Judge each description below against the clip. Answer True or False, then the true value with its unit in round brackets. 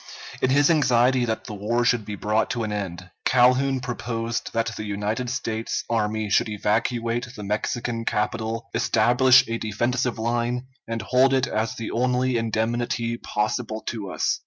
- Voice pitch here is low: True (115 Hz)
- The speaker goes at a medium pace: True (160 wpm)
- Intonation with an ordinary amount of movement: False (2.2 semitones)